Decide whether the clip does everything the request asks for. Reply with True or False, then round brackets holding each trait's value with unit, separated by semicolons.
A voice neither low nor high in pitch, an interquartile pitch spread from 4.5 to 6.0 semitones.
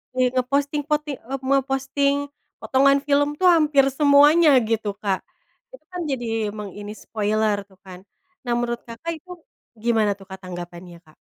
False (255 Hz; 5.4 semitones)